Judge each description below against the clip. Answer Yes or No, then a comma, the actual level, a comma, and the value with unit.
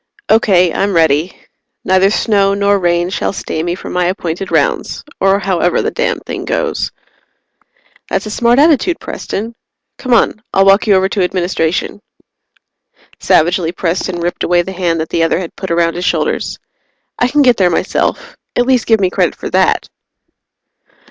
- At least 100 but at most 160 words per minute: No, average, 170 wpm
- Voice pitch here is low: No, high, 190 Hz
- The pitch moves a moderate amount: Yes, average, 3.3 semitones